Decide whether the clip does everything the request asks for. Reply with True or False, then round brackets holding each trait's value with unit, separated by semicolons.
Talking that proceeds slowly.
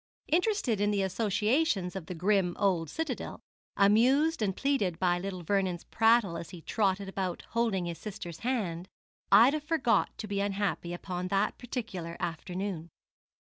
False (145 wpm)